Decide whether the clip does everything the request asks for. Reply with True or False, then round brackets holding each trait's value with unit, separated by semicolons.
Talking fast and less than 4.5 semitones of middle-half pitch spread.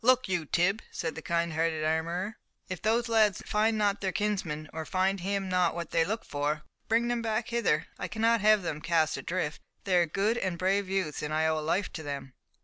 False (220 wpm; 4.8 semitones)